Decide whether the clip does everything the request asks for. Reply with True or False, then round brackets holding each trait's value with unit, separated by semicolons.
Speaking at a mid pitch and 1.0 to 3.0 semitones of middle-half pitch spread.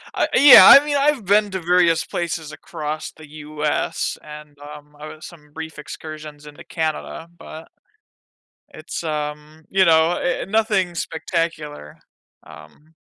True (160 Hz; 2.6 semitones)